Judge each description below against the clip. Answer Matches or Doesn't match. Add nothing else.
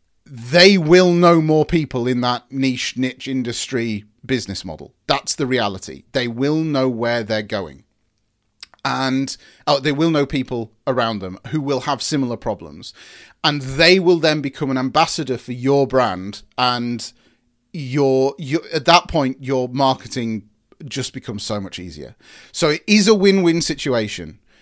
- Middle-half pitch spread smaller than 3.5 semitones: Doesn't match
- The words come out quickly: Doesn't match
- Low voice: Matches